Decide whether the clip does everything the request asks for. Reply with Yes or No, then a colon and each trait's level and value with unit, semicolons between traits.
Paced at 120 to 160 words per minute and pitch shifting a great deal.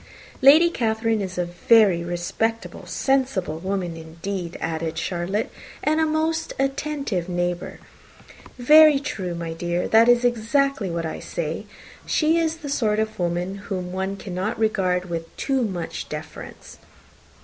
Yes: average, 140 wpm; wide, 6.9 semitones